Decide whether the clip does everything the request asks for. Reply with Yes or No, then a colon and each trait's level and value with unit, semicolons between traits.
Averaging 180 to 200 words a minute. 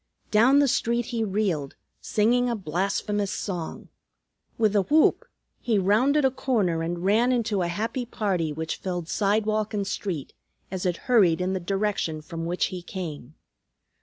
No: average, 160 wpm